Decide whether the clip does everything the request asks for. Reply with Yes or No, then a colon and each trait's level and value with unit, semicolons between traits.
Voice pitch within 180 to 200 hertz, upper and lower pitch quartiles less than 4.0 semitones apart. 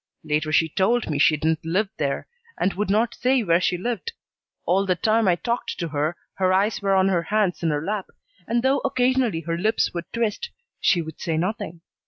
No: high, 190 Hz; average, 5.3 semitones